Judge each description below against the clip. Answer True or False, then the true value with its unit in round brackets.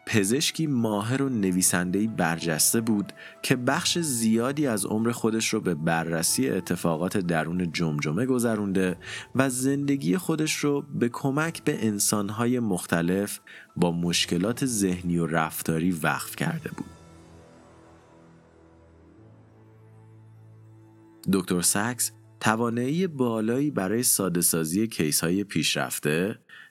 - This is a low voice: True (105 Hz)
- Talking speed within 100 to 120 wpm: True (105 wpm)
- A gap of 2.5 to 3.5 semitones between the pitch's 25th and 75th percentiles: False (5.6 semitones)